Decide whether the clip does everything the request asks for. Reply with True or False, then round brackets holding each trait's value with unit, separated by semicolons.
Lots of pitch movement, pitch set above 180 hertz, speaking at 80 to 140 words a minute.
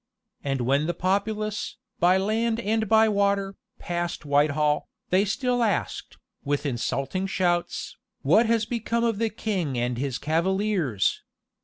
True (6.6 semitones; 190 Hz; 135 wpm)